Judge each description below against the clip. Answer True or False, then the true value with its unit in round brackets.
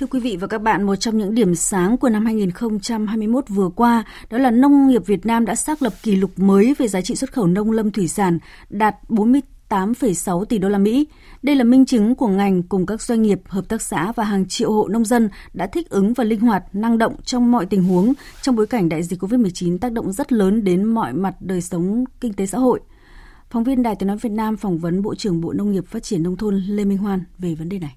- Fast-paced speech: True (255 wpm)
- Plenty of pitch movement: False (3.6 semitones)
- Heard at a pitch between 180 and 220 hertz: True (215 Hz)